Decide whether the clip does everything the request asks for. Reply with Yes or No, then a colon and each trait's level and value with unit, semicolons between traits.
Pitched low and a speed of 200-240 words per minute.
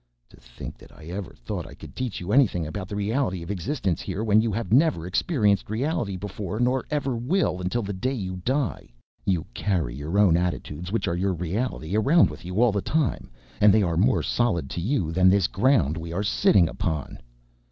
Yes: low, 100 Hz; fast, 205 wpm